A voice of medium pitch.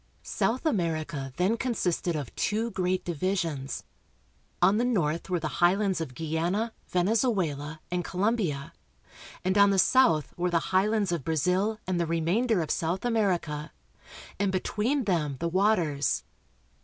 Yes: medium, 180 Hz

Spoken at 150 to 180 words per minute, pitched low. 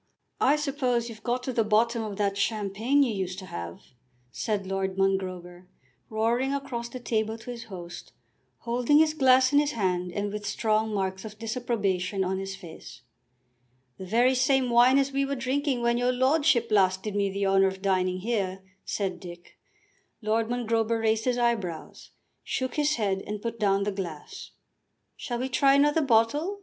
No: average, 175 wpm; high, 220 Hz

